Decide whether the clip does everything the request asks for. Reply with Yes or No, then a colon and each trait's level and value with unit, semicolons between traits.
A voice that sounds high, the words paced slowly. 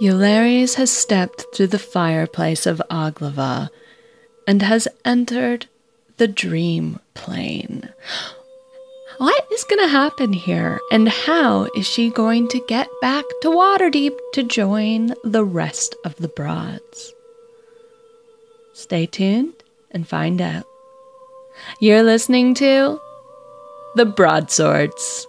Yes: high, 245 Hz; slow, 110 wpm